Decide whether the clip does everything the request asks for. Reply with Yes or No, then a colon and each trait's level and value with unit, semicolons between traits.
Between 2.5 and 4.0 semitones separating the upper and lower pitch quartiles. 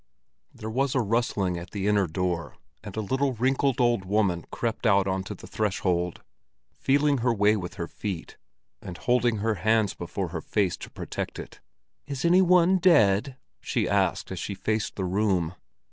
No: average, 4.7 semitones